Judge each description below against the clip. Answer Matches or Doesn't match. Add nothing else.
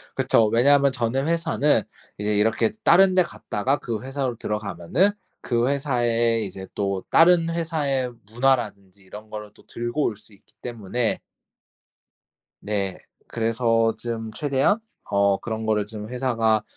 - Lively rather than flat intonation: Doesn't match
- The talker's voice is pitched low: Matches